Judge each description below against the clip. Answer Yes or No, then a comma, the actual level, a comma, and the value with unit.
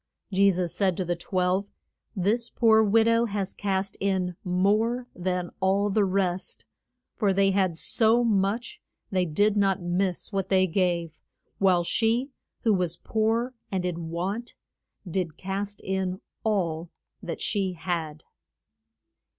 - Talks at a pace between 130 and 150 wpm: Yes, average, 140 wpm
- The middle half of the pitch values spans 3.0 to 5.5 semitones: No, narrow, 2.4 semitones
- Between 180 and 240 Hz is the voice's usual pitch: Yes, high, 190 Hz